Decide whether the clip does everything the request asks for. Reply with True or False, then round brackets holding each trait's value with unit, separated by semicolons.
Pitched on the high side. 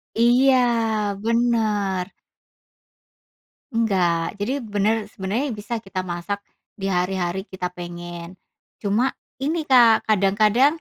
True (205 Hz)